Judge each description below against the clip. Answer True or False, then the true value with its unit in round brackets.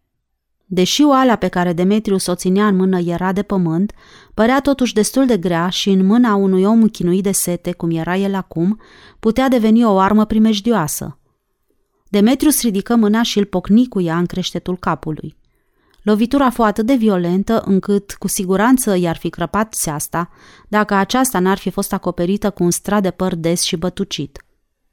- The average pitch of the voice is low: False (195 Hz)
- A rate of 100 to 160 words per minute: False (170 wpm)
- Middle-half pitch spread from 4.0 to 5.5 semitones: False (3.4 semitones)